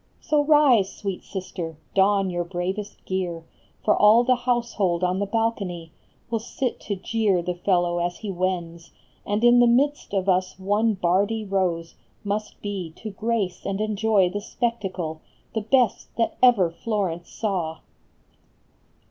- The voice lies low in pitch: No, high, 195 Hz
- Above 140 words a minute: Yes, average, 150 wpm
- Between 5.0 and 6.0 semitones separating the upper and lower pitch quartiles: No, average, 3.9 semitones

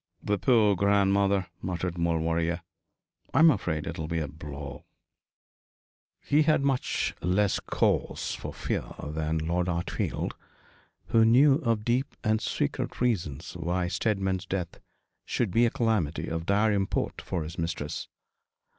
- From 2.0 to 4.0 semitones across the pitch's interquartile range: No, average, 4.9 semitones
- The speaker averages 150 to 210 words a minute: No, slow, 135 wpm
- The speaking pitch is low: Yes, very low, 95 Hz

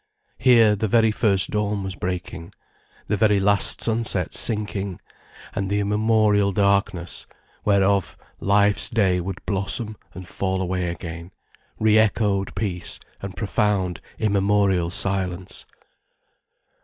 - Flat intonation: Yes, narrow, 2.0 semitones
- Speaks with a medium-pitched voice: No, low, 100 Hz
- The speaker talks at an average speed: No, slow, 115 wpm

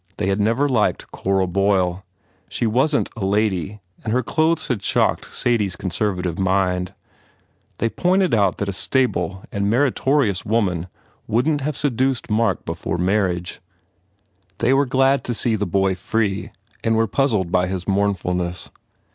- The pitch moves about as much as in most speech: Yes, average, 4.7 semitones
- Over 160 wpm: Yes, average, 170 wpm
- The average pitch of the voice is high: No, low, 105 Hz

